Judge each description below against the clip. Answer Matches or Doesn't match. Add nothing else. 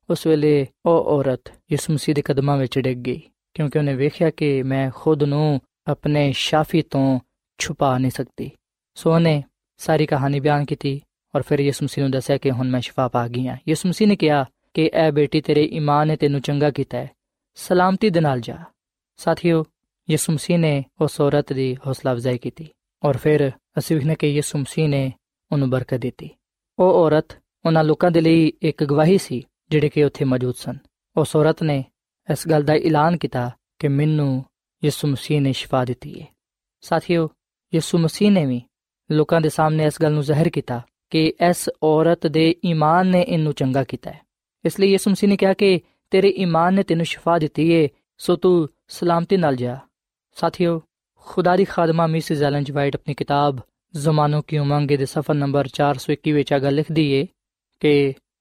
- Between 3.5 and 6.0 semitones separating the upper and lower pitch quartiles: Doesn't match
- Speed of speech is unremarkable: Doesn't match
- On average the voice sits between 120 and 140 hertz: Doesn't match